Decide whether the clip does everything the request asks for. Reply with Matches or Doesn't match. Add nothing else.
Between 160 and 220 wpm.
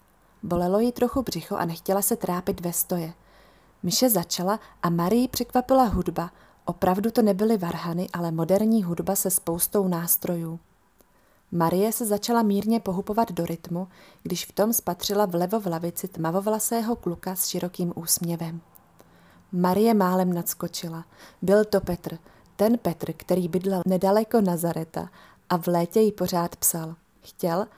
Doesn't match